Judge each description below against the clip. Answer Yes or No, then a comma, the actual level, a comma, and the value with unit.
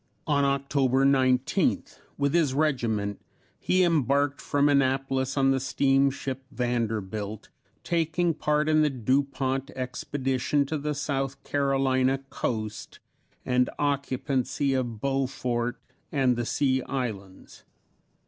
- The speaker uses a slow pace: Yes, slow, 110 wpm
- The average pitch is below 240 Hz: Yes, low, 135 Hz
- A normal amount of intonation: No, narrow, 2.0 semitones